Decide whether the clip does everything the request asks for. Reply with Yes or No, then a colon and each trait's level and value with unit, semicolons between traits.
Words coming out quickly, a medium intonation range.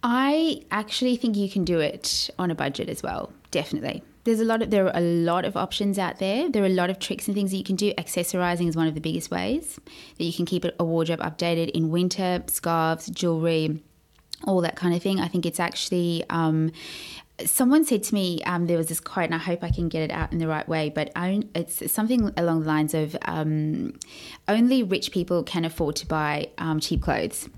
Yes: fast, 230 wpm; average, 3.8 semitones